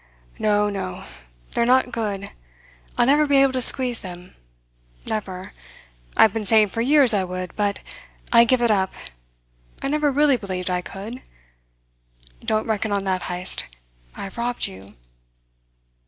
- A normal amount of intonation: Yes, average, 4.5 semitones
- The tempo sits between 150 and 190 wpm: Yes, average, 155 wpm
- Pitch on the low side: No, high, 215 Hz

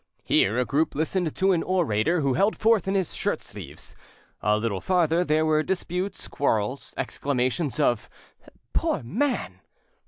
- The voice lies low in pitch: No, medium, 155 Hz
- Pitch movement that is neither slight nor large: No, wide, 6.6 semitones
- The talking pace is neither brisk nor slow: Yes, average, 150 wpm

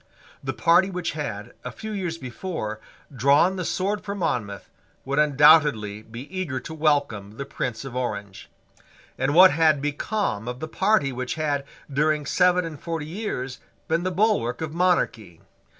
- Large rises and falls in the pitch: Yes, wide, 5.9 semitones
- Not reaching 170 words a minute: Yes, average, 160 wpm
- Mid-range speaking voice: Yes, medium, 150 Hz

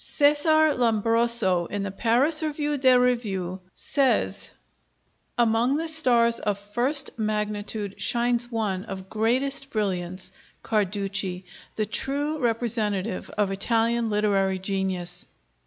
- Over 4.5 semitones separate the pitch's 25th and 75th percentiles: No, average, 4.1 semitones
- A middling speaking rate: No, slow, 105 wpm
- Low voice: No, high, 225 Hz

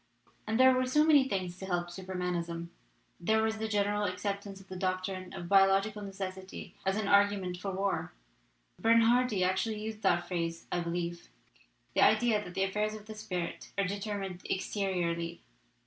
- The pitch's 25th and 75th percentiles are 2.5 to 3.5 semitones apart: Yes, average, 2.8 semitones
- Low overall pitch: No, high, 195 Hz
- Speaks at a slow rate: No, average, 165 wpm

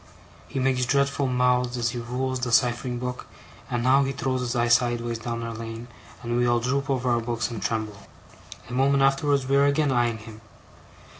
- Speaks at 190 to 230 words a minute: Yes, average, 200 wpm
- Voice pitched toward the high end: No, low, 125 Hz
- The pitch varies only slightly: Yes, narrow, 2.1 semitones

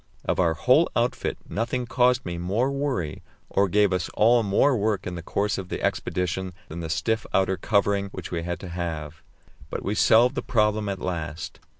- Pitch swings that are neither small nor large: Yes, average, 4.3 semitones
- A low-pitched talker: Yes, low, 100 Hz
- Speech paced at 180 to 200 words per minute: Yes, average, 195 wpm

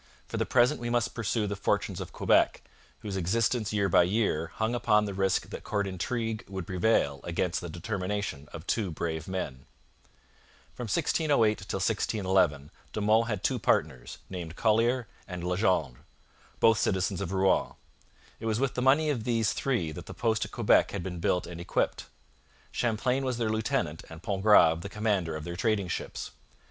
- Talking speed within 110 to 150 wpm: No, average, 175 wpm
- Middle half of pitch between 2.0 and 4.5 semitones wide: Yes, average, 4.2 semitones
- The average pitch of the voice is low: Yes, low, 100 Hz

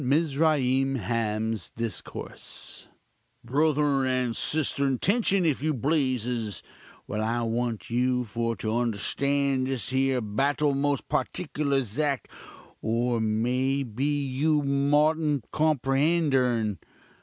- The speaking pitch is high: No, low, 135 Hz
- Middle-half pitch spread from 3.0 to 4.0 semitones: Yes, average, 3.7 semitones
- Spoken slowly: Yes, slow, 105 wpm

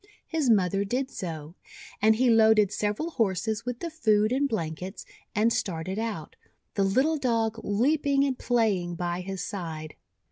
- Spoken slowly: No, average, 150 wpm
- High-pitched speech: Yes, high, 215 Hz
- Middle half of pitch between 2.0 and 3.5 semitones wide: No, average, 5.0 semitones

